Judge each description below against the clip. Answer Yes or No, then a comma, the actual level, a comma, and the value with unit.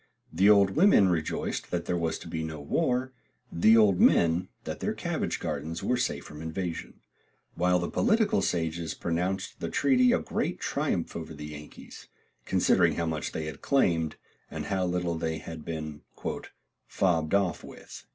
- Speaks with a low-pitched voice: Yes, very low, 85 Hz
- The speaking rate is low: No, average, 165 wpm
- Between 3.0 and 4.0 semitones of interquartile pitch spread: Yes, average, 3.4 semitones